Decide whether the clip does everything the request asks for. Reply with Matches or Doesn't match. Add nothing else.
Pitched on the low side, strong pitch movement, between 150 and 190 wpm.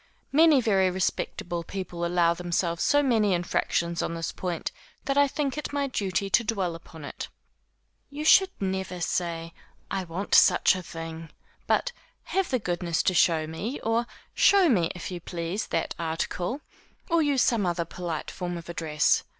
Doesn't match